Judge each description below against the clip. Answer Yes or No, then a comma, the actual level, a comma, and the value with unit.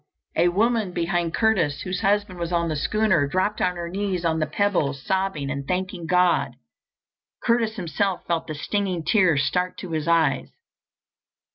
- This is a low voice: No, medium, 180 Hz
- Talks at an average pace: Yes, average, 160 wpm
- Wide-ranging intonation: No, average, 3.2 semitones